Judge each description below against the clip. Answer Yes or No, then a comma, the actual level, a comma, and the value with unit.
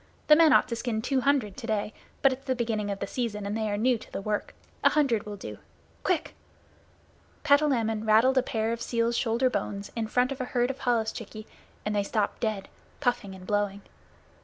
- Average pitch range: Yes, average, 3.4 semitones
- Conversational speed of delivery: No, fast, 210 wpm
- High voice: Yes, high, 230 Hz